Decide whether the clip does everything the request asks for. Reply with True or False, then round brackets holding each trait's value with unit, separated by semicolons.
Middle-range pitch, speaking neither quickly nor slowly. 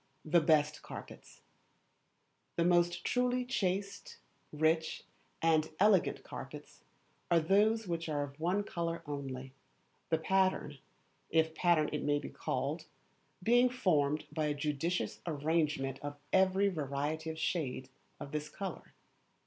False (160 Hz; 125 wpm)